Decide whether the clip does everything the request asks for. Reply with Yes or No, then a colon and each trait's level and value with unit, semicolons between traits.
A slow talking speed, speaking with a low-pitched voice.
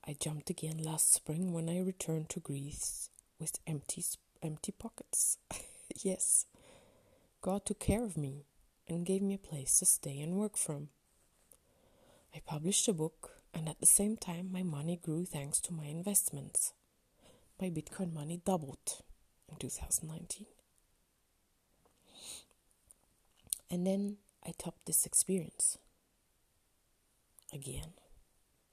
No: slow, 125 wpm; medium, 170 Hz